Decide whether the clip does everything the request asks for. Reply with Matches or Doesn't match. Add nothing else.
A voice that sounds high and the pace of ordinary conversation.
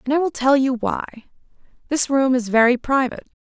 Matches